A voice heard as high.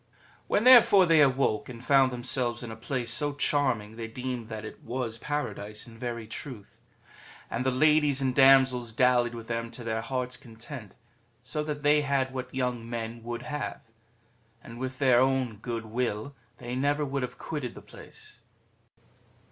No: low, 125 Hz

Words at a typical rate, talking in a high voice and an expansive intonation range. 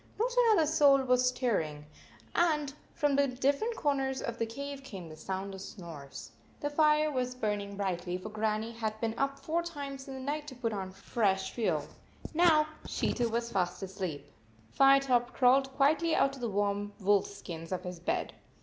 Yes: average, 180 wpm; high, 245 Hz; wide, 6.0 semitones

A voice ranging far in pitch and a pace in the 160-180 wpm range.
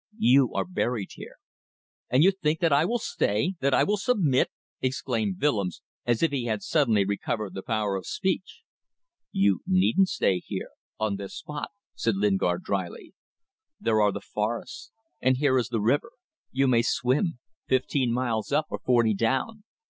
Yes: wide, 5.9 semitones; average, 165 wpm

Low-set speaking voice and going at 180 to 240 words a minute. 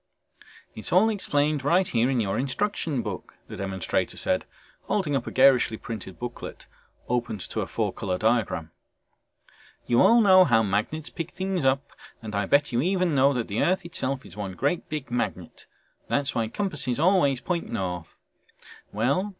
No: low, 130 Hz; average, 165 wpm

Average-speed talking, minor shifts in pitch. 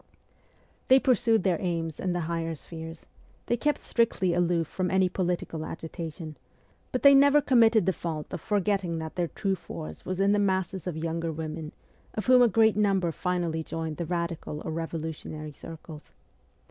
No: average, 170 wpm; average, 3.5 semitones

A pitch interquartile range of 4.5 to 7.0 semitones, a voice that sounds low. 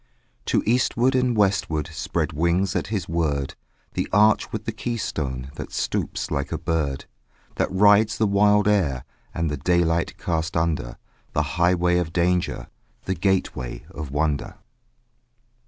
Yes: average, 5.1 semitones; very low, 85 Hz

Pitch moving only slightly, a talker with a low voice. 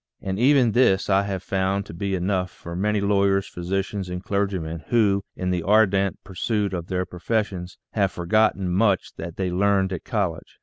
Yes: narrow, 1.9 semitones; very low, 95 Hz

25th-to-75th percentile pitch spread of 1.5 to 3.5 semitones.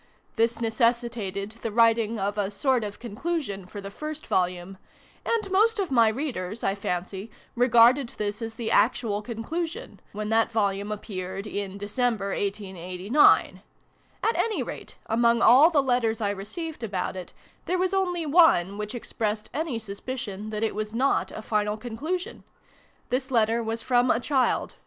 No: average, 4.0 semitones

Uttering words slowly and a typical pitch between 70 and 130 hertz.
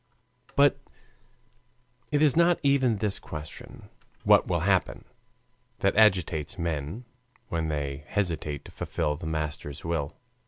Yes: slow, 120 wpm; very low, 85 Hz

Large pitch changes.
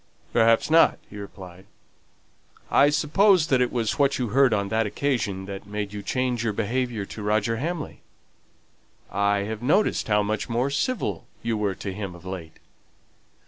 No: average, 4.3 semitones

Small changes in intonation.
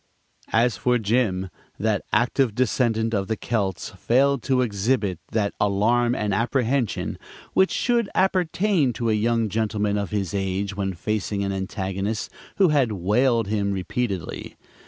No: average, 3.7 semitones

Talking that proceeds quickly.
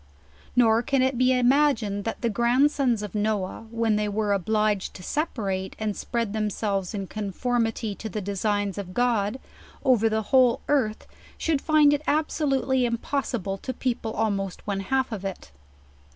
No: average, 160 wpm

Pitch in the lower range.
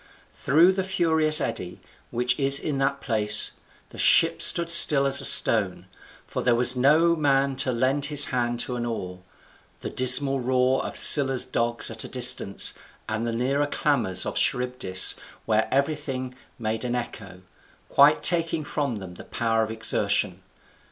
Yes: low, 130 Hz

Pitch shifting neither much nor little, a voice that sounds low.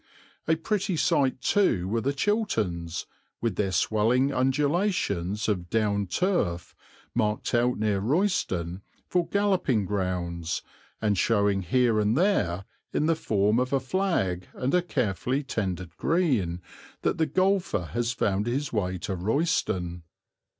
No: wide, 8.0 semitones; low, 115 Hz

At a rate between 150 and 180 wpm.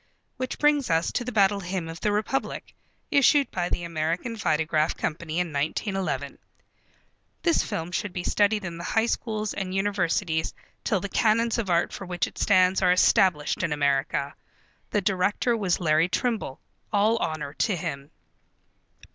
Yes: average, 160 wpm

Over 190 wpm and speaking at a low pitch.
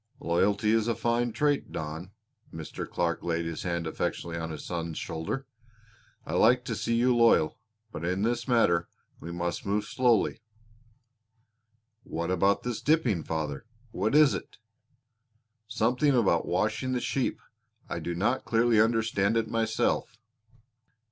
No: average, 140 wpm; low, 105 Hz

